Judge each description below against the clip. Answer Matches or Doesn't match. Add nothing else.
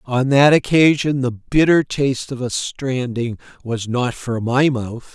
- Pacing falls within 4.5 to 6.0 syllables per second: Doesn't match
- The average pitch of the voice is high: Doesn't match